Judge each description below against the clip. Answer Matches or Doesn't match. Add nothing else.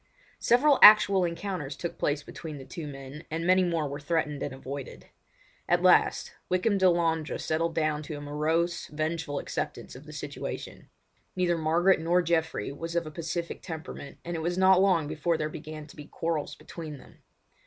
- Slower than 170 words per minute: Doesn't match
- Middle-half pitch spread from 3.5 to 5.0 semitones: Doesn't match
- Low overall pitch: Doesn't match